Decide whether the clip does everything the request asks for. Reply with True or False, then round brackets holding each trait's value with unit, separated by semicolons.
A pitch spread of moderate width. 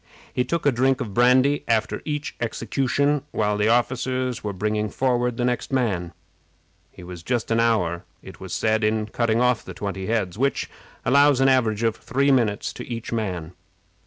True (3.5 semitones)